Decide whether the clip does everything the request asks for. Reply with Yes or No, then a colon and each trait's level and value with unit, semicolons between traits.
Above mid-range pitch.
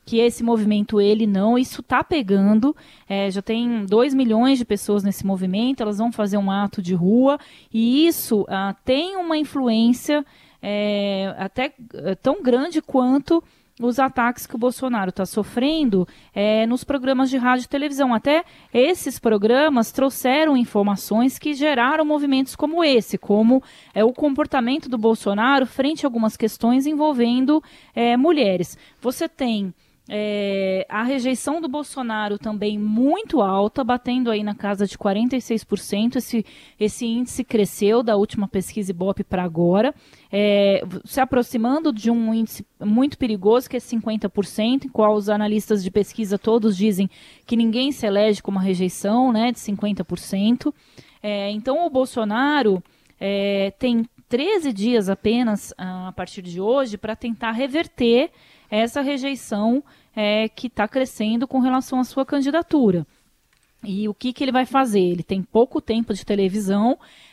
Yes: high, 230 Hz